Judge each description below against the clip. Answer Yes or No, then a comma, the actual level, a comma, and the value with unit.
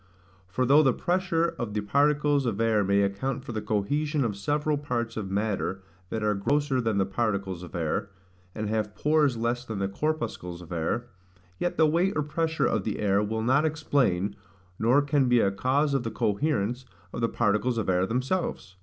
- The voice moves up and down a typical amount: No, wide, 6.2 semitones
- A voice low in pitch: Yes, low, 115 Hz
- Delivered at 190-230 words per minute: Yes, average, 195 wpm